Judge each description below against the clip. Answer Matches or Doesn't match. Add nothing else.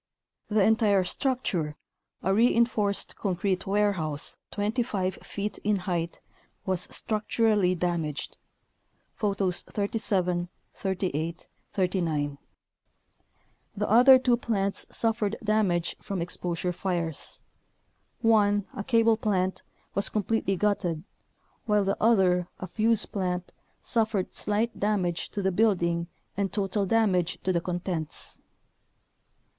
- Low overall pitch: Doesn't match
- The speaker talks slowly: Matches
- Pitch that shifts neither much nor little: Matches